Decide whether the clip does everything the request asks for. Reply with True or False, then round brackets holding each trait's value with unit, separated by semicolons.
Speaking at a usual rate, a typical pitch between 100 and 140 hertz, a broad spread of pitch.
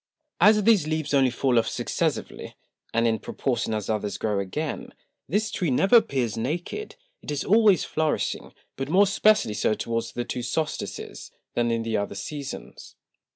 True (160 wpm; 135 Hz; 7.5 semitones)